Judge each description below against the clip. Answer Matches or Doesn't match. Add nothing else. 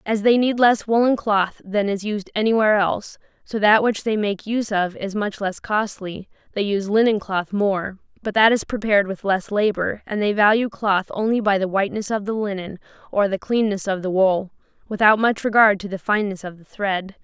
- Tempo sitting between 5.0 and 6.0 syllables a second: Matches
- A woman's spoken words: Matches